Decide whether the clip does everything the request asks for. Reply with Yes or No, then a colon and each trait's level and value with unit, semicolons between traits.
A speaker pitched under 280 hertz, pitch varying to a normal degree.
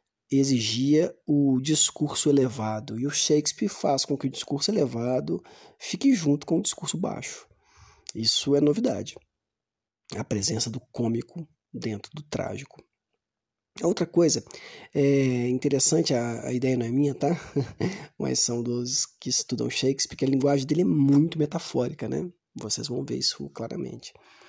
Yes: low, 135 Hz; average, 3.9 semitones